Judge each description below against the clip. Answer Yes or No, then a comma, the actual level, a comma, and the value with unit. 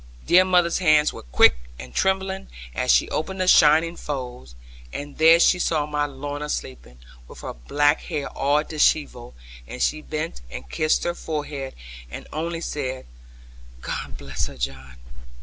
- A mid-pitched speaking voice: Yes, medium, 150 Hz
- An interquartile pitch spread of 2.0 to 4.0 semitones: No, average, 5.3 semitones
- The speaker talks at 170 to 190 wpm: No, average, 155 wpm